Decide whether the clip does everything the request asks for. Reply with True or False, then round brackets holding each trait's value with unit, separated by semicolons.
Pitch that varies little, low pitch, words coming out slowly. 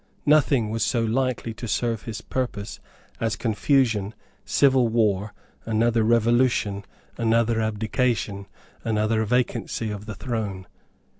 True (2.0 semitones; 115 Hz; 115 wpm)